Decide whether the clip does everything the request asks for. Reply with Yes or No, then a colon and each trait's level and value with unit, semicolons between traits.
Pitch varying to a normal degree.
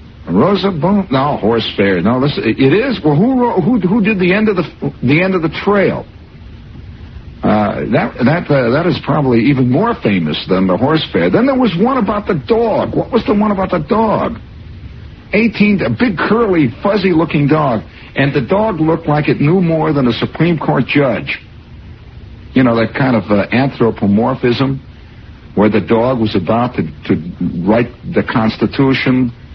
No: wide, 9.0 semitones